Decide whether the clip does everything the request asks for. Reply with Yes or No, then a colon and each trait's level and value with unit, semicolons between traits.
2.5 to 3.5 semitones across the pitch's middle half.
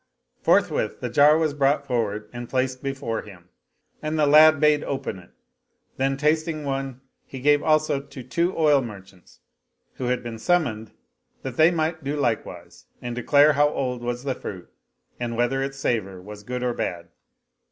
No: average, 4.0 semitones